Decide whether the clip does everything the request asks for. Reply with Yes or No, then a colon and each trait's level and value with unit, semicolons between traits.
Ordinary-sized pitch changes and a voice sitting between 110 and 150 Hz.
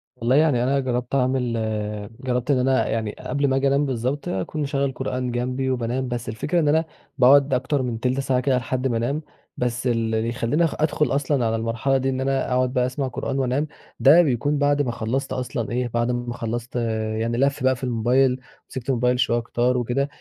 No: narrow, 2.2 semitones; low, 125 Hz